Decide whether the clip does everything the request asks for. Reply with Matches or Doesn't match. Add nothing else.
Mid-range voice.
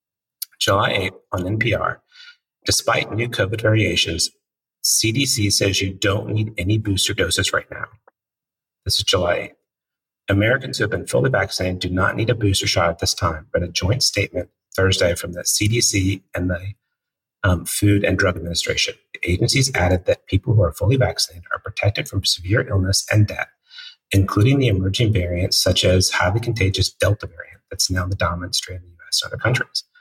Doesn't match